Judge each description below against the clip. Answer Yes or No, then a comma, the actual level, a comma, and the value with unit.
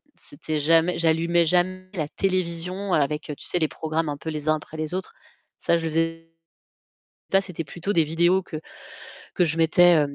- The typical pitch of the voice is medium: Yes, medium, 165 Hz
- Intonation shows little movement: Yes, narrow, 2.2 semitones